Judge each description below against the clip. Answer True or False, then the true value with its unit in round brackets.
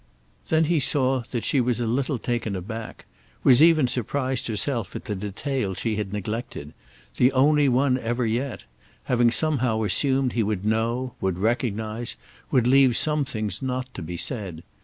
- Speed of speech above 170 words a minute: False (160 wpm)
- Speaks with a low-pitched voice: True (120 Hz)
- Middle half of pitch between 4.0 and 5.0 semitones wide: False (3.6 semitones)